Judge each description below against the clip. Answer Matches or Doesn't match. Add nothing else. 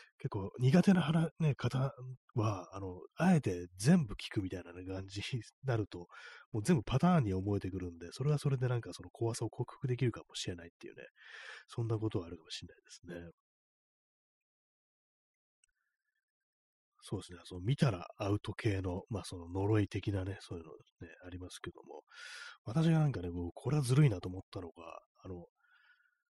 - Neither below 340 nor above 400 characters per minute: Matches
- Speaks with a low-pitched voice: Matches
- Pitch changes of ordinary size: Doesn't match